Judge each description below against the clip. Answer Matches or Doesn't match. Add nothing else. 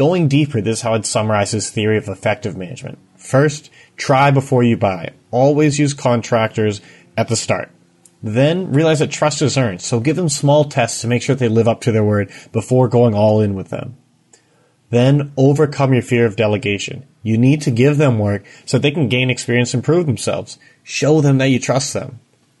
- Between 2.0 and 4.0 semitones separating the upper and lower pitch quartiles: Doesn't match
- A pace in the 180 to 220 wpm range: Matches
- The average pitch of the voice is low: Matches